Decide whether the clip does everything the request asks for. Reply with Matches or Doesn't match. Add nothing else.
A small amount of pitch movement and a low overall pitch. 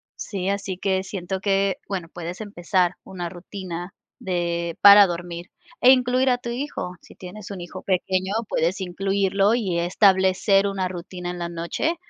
Doesn't match